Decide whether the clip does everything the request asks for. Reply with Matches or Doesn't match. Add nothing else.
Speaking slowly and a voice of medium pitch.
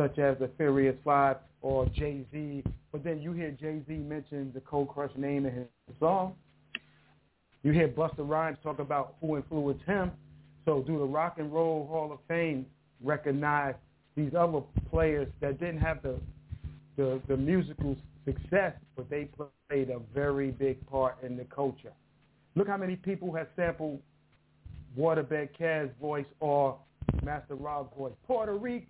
Doesn't match